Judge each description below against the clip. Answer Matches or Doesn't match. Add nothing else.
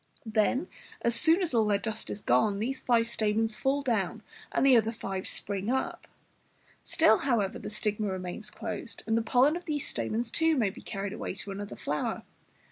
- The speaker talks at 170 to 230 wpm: Matches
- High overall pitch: Matches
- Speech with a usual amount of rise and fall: Matches